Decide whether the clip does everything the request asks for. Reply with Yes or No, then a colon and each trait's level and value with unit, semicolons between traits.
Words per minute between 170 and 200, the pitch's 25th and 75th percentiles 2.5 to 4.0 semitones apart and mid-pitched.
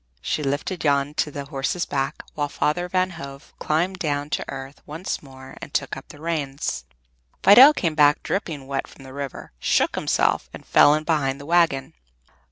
Yes: average, 180 wpm; average, 3.2 semitones; medium, 145 Hz